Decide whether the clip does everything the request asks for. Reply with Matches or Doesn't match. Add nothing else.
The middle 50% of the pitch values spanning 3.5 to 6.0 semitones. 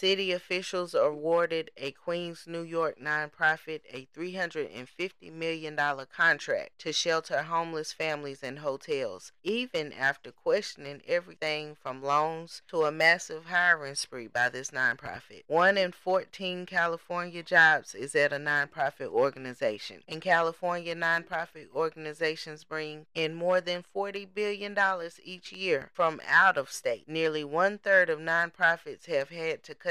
Doesn't match